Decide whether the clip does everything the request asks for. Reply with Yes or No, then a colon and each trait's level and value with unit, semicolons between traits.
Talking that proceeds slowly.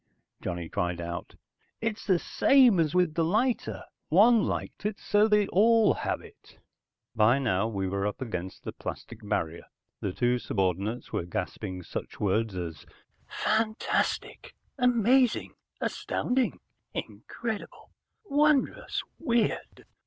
Yes: slow, 125 wpm